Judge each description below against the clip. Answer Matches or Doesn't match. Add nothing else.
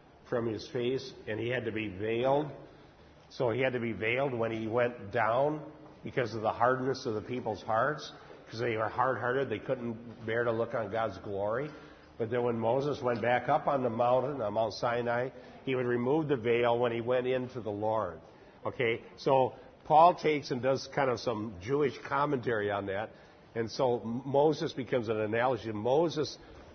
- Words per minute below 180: Doesn't match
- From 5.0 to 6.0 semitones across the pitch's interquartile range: Doesn't match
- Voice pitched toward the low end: Matches